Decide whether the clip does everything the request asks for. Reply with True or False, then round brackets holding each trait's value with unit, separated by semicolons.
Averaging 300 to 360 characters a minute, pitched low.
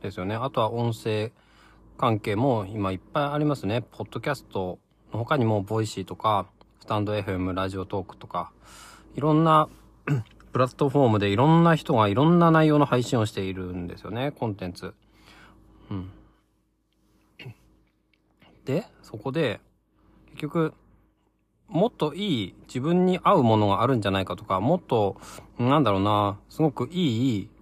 True (305 characters per minute; 110 Hz)